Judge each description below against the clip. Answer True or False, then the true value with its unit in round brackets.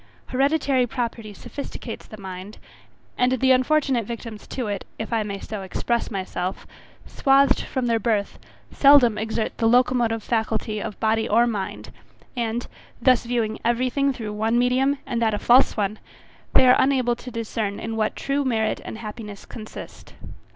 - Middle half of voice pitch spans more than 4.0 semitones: False (2.8 semitones)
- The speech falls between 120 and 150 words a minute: False (160 wpm)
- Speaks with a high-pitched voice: True (230 Hz)